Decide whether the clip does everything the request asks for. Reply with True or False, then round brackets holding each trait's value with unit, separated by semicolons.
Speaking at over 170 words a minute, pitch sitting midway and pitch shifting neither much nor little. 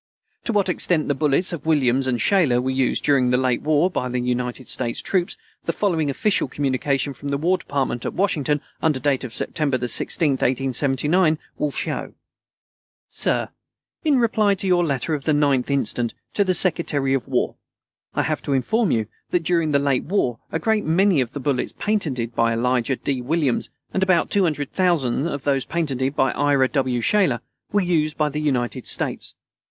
True (180 wpm; 145 Hz; 4.7 semitones)